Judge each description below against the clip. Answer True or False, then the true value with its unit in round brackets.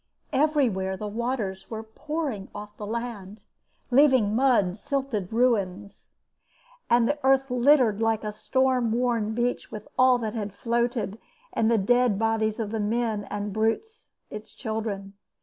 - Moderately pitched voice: False (225 Hz)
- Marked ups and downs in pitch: False (3.1 semitones)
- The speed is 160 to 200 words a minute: False (145 wpm)